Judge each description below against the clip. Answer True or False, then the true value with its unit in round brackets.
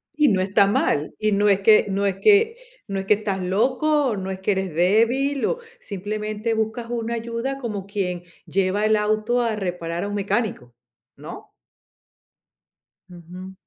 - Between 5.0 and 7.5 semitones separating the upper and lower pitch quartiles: False (3.4 semitones)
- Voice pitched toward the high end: True (210 Hz)